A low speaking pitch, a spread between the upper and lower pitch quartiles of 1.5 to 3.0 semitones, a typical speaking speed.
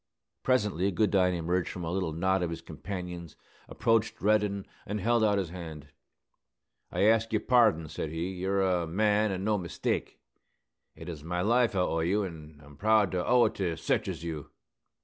No: very low, 95 Hz; average, 3.9 semitones; average, 190 wpm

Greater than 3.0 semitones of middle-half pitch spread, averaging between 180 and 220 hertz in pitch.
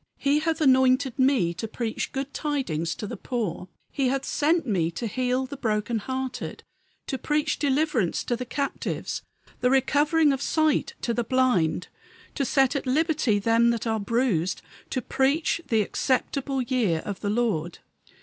No: average, 4.0 semitones; very high, 255 Hz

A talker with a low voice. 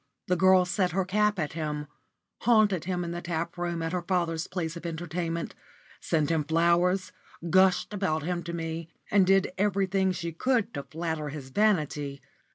No: medium, 175 Hz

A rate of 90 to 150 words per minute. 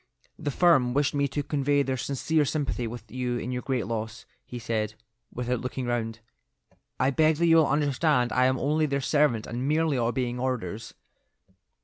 No: average, 175 wpm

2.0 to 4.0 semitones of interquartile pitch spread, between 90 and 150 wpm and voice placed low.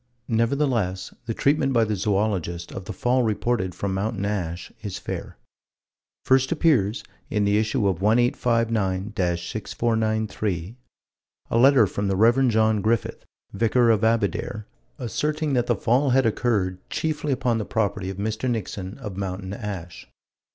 Yes: average, 3.7 semitones; average, 145 wpm; low, 110 Hz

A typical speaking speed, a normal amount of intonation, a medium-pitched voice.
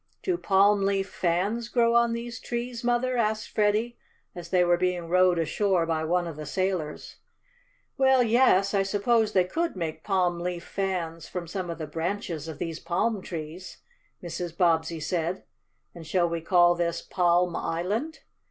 Yes: average, 165 wpm; average, 4.0 semitones; medium, 180 Hz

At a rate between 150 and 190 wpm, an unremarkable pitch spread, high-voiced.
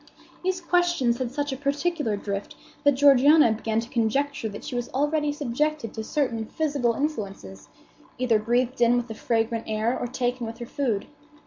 Yes: average, 175 wpm; average, 4.2 semitones; high, 245 Hz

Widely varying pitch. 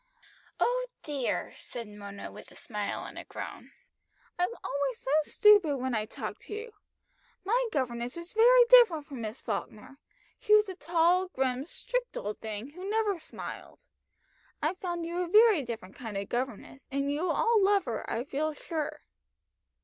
Yes: wide, 8.4 semitones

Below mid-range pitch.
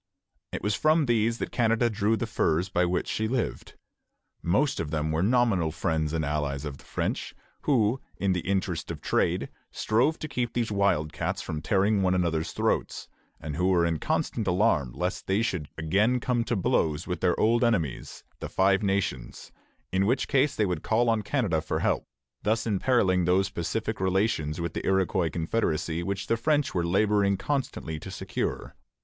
Yes: very low, 95 Hz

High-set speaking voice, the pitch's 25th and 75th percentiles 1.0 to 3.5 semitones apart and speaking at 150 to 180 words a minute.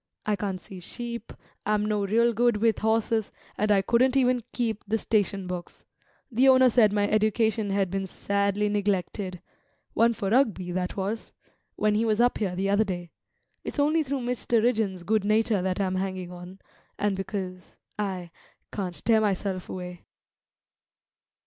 Yes: high, 205 Hz; average, 3.1 semitones; average, 160 wpm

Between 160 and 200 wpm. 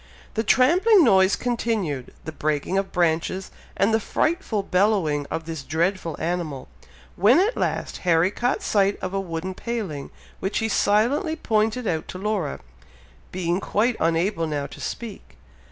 No: average, 150 wpm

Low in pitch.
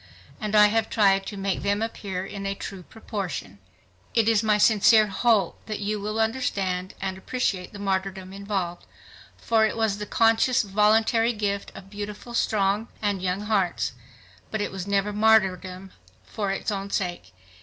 No: high, 205 Hz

